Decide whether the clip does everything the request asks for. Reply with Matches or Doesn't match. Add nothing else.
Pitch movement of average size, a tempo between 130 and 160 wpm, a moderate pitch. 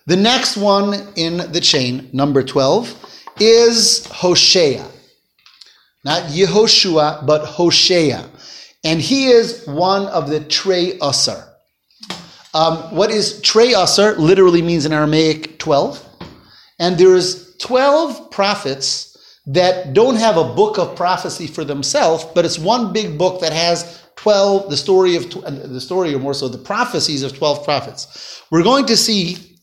Matches